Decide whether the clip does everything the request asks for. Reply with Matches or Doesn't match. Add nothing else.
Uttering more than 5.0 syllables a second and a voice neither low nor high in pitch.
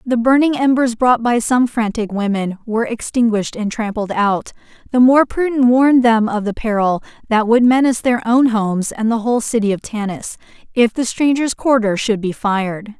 Doesn't match